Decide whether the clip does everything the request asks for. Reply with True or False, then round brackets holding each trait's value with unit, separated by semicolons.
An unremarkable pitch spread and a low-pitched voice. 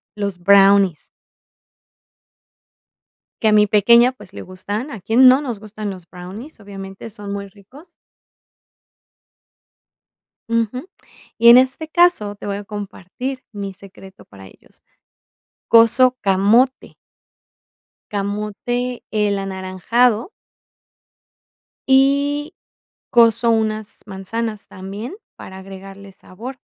False (3.8 semitones; 210 Hz)